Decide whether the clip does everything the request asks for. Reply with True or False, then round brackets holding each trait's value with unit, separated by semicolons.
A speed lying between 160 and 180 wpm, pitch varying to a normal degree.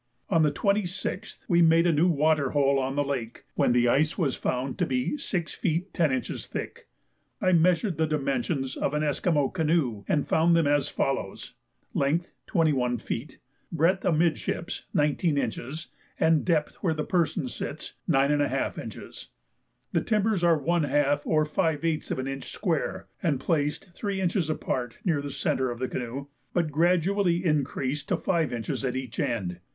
True (170 wpm; 3.9 semitones)